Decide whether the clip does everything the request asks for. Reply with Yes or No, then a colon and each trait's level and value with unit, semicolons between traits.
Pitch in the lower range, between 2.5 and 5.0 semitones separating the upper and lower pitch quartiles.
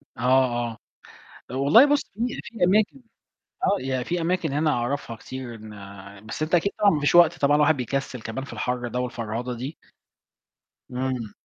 No: low, 130 Hz; wide, 5.4 semitones